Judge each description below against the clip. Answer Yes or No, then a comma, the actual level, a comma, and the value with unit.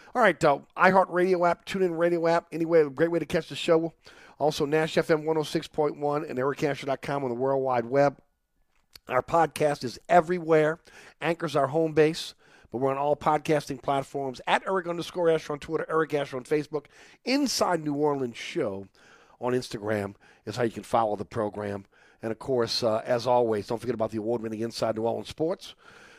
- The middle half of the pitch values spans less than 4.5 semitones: No, average, 5.0 semitones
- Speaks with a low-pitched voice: No, medium, 145 Hz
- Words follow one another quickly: No, average, 185 wpm